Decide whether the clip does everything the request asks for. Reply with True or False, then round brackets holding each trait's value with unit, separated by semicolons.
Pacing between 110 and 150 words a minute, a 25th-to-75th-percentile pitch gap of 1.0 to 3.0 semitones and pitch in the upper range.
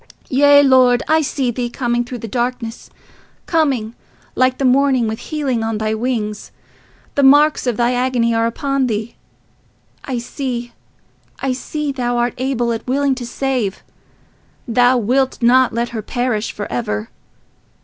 True (145 wpm; 2.4 semitones; 245 Hz)